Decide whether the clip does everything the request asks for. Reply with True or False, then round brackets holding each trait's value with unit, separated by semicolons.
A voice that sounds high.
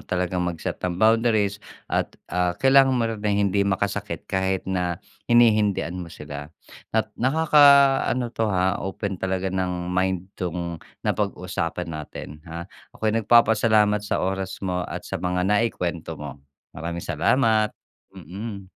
False (95 Hz)